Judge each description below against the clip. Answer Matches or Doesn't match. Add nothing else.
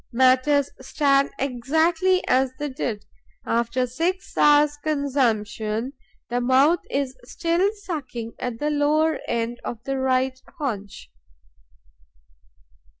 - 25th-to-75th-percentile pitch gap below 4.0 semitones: Matches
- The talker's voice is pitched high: Matches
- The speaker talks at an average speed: Doesn't match